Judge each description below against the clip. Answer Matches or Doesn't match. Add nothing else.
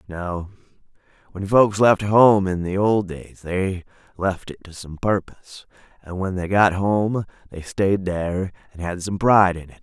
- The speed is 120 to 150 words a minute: Doesn't match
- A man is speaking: Matches